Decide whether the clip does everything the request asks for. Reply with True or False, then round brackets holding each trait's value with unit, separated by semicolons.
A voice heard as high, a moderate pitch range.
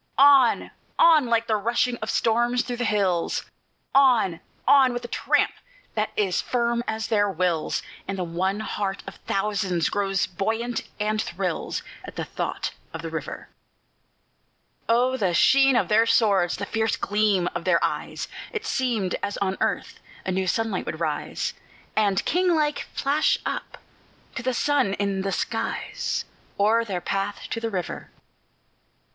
True (215 Hz; 3.9 semitones)